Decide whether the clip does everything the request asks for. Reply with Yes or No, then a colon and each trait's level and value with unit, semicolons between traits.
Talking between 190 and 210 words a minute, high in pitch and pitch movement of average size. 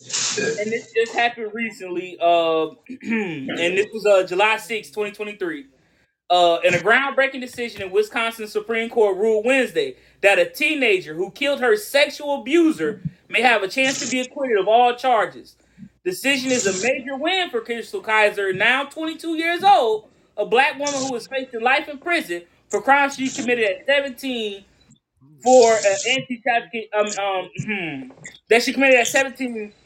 No: average, 160 wpm; high, 235 Hz; average, 4.9 semitones